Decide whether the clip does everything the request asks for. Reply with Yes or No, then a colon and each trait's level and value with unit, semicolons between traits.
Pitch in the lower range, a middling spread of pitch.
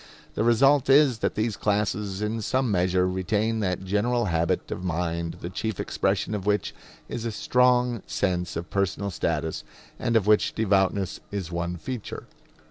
Yes: low, 100 Hz; average, 3.8 semitones